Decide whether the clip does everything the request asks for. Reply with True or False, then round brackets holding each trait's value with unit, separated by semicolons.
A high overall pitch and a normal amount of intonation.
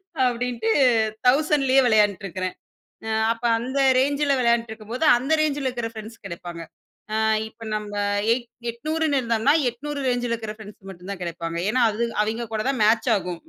True (235 Hz; 3.5 semitones)